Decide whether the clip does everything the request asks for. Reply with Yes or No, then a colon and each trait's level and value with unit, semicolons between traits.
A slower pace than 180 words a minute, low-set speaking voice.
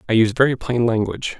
No: fast, 215 wpm; low, 120 Hz